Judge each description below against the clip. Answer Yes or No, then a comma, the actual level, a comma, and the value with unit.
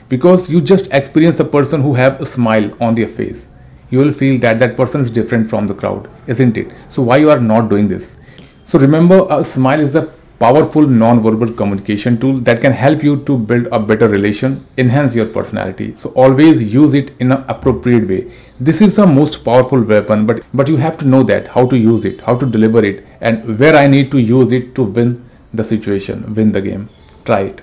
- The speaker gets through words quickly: Yes, fast, 215 wpm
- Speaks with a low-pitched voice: Yes, low, 125 Hz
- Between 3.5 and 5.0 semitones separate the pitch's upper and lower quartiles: Yes, average, 4.1 semitones